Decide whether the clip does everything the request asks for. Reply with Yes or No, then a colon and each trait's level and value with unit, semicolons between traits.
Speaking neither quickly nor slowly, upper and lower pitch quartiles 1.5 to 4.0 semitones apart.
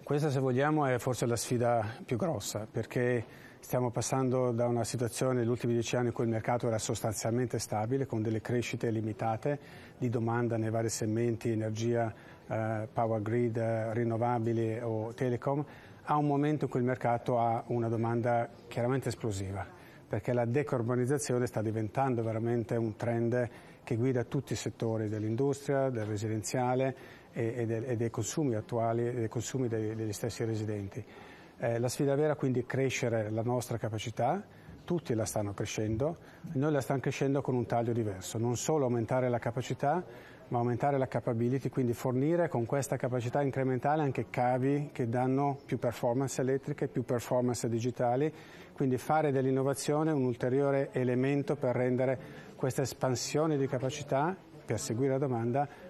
Yes: average, 155 wpm; average, 2.7 semitones